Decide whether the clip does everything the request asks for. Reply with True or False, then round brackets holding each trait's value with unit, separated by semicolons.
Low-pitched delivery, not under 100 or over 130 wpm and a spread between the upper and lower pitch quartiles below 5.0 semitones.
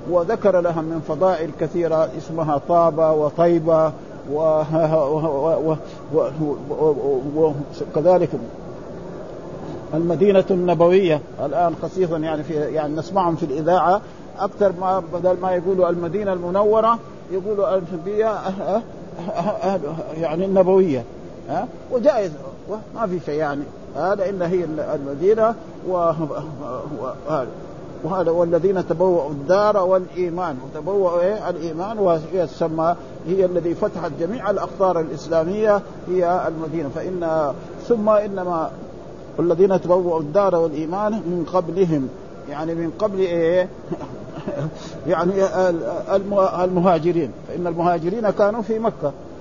False (175 Hz; 110 wpm; 2.7 semitones)